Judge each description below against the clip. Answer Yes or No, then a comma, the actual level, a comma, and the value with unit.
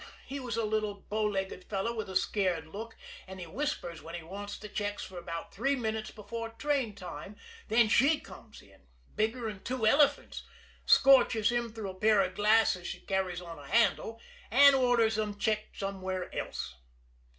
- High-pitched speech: Yes, high, 210 Hz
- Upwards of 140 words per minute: Yes, average, 175 wpm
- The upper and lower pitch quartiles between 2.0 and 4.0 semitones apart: Yes, average, 3.4 semitones